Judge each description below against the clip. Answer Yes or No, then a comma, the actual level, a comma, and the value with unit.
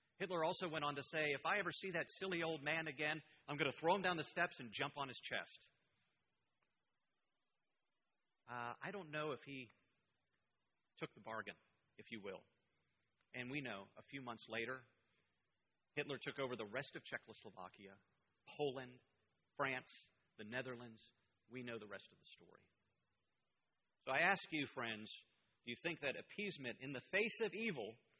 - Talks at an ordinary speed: Yes, average, 170 wpm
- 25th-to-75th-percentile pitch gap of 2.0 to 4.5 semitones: No, average, 5.1 semitones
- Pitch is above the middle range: No, medium, 140 Hz